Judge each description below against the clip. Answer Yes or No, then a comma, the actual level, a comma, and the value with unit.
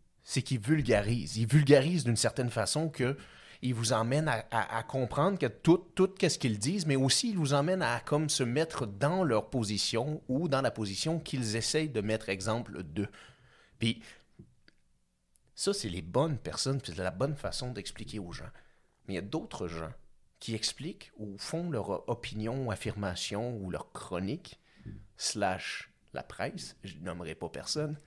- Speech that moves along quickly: No, average, 175 wpm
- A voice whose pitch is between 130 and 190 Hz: No, low, 120 Hz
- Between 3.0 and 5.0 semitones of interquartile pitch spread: No, wide, 5.5 semitones